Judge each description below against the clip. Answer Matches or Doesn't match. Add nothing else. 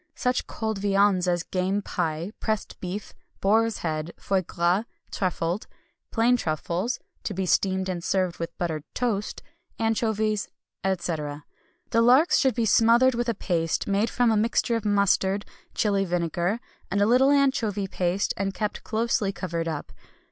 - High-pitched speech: Matches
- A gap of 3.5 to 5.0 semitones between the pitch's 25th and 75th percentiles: Matches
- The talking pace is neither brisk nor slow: Matches